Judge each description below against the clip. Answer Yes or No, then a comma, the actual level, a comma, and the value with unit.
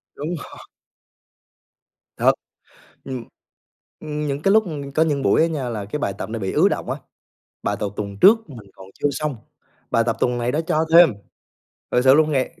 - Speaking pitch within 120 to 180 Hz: Yes, medium, 140 Hz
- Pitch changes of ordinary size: Yes, average, 4.6 semitones